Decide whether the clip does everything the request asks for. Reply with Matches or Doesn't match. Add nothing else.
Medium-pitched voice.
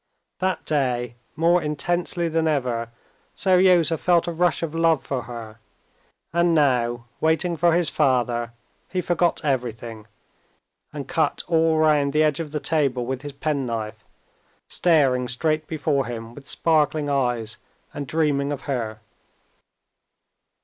Matches